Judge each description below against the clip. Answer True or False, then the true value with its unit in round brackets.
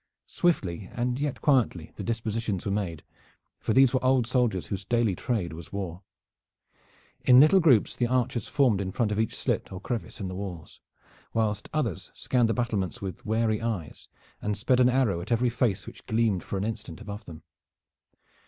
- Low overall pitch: True (110 Hz)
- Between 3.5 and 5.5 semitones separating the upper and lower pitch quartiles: True (4.2 semitones)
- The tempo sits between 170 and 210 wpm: True (180 wpm)